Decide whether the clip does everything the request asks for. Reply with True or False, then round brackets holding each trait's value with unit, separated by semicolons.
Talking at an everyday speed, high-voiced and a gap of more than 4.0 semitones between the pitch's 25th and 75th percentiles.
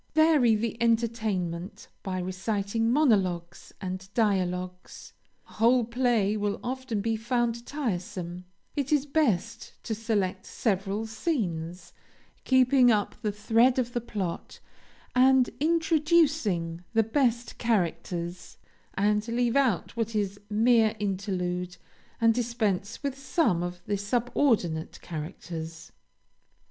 False (110 wpm; 220 Hz; 4.7 semitones)